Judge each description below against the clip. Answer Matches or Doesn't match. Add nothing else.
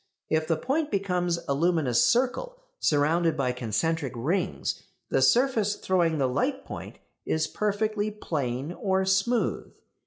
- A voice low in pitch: Doesn't match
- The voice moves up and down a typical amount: Doesn't match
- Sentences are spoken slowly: Matches